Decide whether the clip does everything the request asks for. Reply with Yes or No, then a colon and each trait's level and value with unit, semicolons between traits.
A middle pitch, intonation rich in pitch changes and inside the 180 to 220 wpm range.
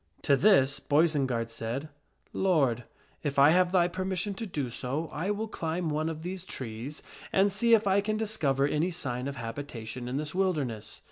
Yes: medium, 155 Hz; wide, 6.0 semitones; average, 190 wpm